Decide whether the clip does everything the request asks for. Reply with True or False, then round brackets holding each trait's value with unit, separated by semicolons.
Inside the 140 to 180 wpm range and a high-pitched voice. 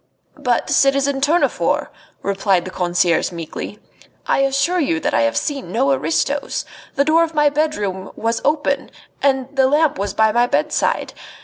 True (155 wpm; 265 Hz)